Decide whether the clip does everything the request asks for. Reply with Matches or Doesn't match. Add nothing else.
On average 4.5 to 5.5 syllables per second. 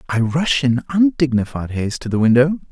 Matches